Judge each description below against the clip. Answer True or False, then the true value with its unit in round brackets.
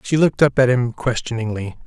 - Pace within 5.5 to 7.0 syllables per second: True (5.9 syllables/s)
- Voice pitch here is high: False (125 Hz)